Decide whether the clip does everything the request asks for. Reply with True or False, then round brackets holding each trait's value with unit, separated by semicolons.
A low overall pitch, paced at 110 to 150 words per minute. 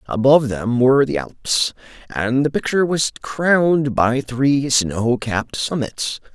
True (130 Hz; 140 wpm)